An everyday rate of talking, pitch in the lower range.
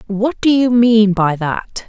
No: average, 190 wpm; high, 220 Hz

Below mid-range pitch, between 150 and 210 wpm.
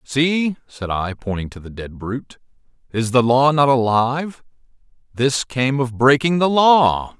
Yes: low, 130 Hz; average, 160 wpm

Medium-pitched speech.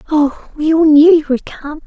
No: very high, 305 Hz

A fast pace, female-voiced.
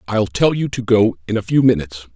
No: fast, 250 wpm; male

